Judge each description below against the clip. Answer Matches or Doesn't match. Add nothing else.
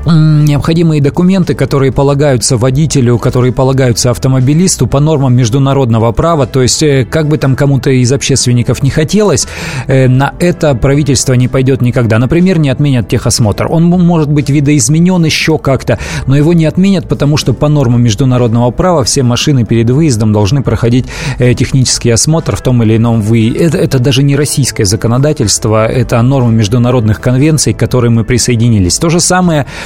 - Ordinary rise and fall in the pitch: Matches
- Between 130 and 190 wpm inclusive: Matches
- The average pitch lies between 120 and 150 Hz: Matches